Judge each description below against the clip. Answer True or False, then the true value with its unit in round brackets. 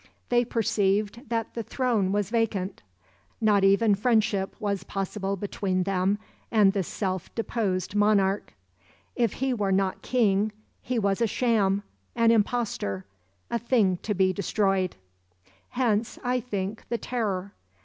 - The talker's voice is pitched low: False (205 Hz)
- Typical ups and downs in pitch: True (3.0 semitones)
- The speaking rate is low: True (130 wpm)